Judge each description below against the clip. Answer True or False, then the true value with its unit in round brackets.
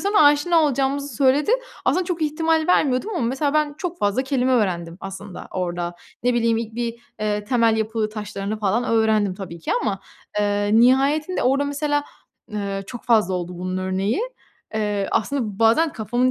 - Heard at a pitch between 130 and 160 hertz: False (230 Hz)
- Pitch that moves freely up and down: True (5.7 semitones)